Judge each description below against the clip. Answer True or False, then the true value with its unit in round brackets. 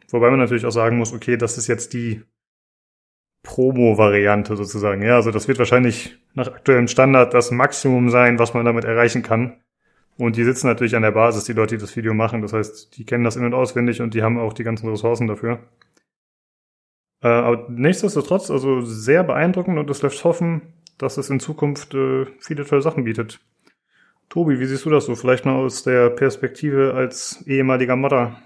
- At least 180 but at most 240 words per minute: True (190 wpm)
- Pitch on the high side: False (120 Hz)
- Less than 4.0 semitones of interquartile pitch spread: True (2.4 semitones)